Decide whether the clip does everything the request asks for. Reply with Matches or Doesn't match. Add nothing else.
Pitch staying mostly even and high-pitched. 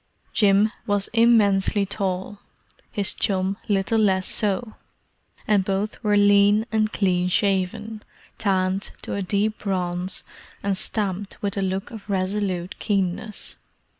Matches